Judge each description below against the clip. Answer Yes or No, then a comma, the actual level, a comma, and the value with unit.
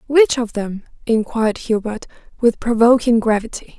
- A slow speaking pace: Yes, slow, 125 wpm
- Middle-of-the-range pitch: No, high, 230 Hz